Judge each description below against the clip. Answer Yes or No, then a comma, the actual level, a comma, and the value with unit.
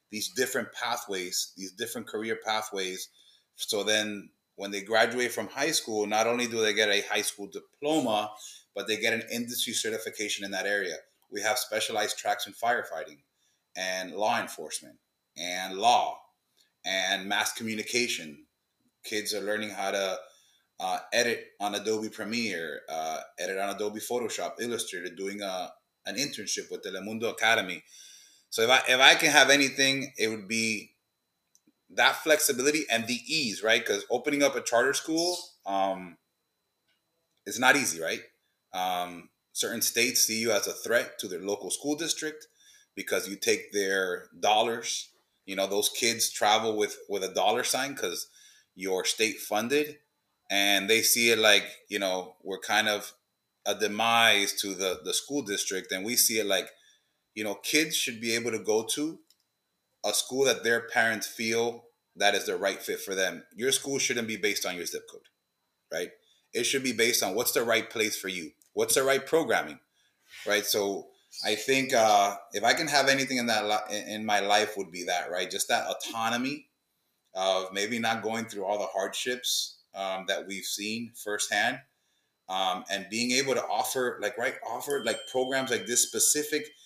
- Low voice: Yes, low, 110 Hz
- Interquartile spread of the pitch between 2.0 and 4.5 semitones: No, average, 5.0 semitones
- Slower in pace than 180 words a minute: Yes, average, 170 wpm